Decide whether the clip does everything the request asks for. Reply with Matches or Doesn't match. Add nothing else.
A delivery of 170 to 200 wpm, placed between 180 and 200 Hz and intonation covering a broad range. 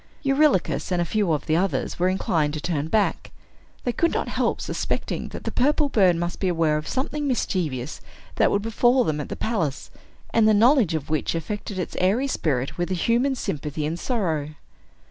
Matches